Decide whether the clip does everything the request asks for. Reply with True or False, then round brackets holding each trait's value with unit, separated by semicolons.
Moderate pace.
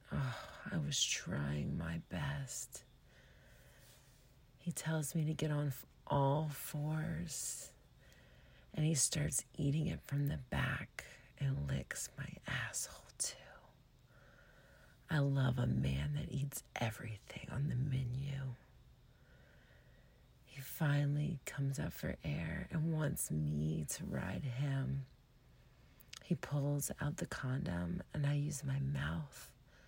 False (120 wpm)